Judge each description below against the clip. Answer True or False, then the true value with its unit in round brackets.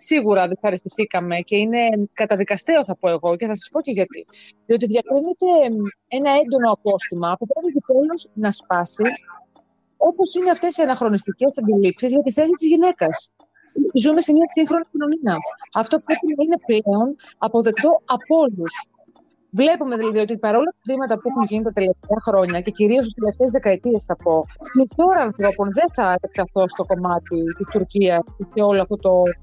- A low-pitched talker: False (225 Hz)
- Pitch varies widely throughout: True (7.1 semitones)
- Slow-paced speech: False (165 wpm)